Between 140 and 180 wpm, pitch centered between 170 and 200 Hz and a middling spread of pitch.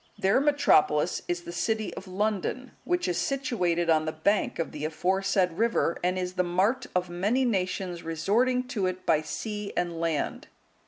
Yes: average, 170 wpm; medium, 185 Hz; average, 4.0 semitones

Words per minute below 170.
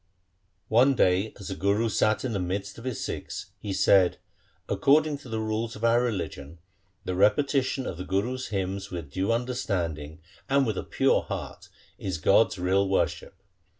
No: average, 180 wpm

